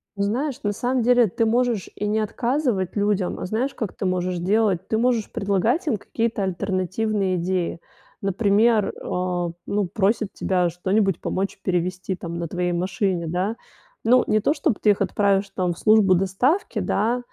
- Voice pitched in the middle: No, high, 200 Hz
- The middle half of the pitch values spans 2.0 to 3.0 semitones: No, average, 3.5 semitones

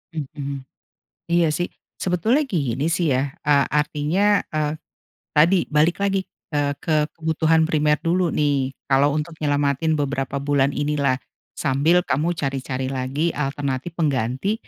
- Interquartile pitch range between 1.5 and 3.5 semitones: Yes, average, 2.9 semitones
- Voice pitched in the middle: Yes, medium, 150 Hz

